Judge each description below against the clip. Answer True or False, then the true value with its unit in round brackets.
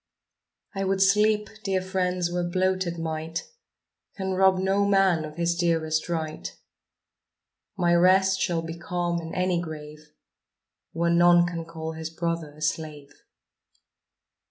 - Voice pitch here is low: False (175 Hz)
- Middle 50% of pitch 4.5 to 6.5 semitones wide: False (2.4 semitones)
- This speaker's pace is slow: True (130 wpm)